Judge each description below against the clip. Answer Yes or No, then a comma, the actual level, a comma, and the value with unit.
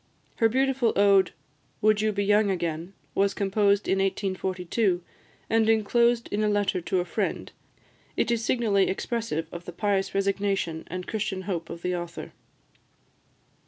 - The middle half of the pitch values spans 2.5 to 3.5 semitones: Yes, average, 2.8 semitones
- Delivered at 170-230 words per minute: No, average, 150 wpm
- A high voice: Yes, high, 200 Hz